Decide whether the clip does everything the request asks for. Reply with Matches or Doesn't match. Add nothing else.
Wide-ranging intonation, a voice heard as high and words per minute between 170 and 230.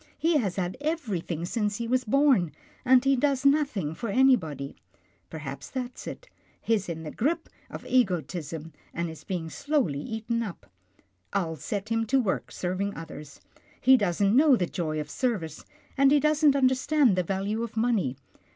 Matches